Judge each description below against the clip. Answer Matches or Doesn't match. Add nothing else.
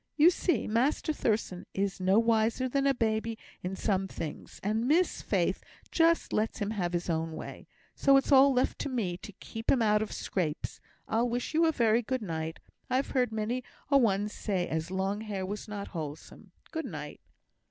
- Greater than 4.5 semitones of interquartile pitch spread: Matches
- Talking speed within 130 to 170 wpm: Doesn't match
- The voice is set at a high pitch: Matches